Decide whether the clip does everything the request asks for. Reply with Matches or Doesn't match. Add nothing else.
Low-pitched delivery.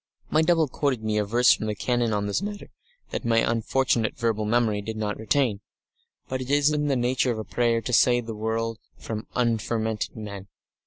Matches